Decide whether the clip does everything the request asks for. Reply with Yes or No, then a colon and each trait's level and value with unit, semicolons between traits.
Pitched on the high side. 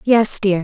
Yes: high, 205 Hz